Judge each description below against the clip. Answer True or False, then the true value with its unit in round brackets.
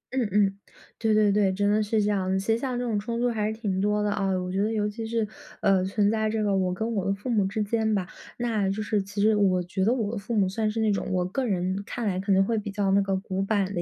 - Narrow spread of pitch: True (2.2 semitones)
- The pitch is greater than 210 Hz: False (205 Hz)